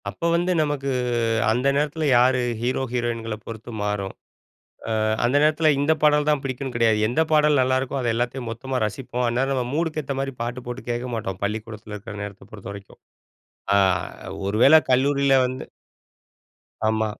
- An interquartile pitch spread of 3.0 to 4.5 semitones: Yes, average, 3.7 semitones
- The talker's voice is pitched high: No, low, 125 Hz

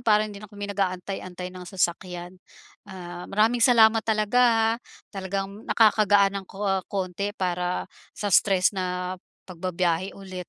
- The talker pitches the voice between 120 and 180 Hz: No, high, 195 Hz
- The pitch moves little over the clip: Yes, narrow, 2.3 semitones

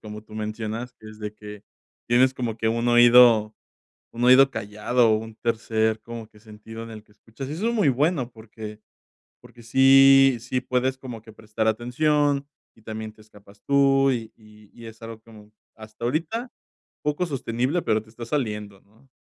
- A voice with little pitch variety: No, average, 3.3 semitones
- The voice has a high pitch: No, low, 115 Hz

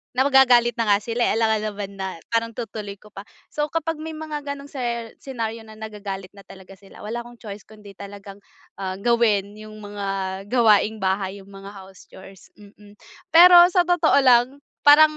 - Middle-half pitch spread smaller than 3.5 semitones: No, average, 4.0 semitones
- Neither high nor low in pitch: No, high, 215 Hz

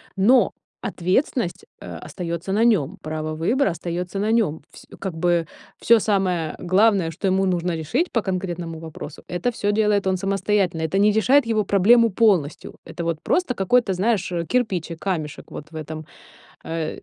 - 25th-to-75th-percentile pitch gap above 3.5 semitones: Yes, average, 4.2 semitones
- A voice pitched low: No, high, 190 Hz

